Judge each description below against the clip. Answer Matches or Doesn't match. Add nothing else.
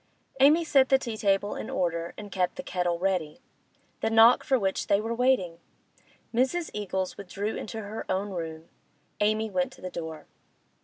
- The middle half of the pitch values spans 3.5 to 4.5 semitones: Matches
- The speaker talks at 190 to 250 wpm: Doesn't match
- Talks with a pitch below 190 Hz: Doesn't match